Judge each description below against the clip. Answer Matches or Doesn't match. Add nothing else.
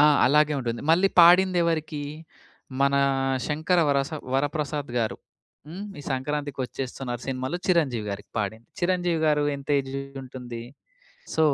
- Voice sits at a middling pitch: Matches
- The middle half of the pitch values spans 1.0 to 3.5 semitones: Doesn't match